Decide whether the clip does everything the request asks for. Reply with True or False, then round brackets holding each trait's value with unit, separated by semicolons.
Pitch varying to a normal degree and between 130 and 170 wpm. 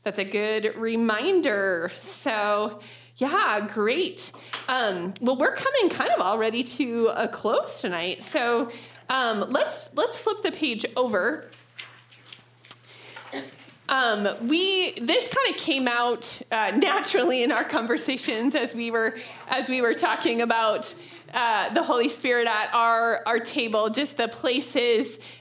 True (4.2 semitones; 135 wpm)